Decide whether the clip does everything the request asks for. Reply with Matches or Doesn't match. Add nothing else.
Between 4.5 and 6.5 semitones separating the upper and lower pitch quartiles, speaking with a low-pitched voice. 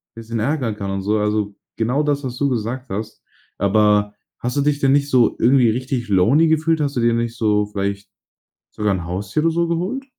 Matches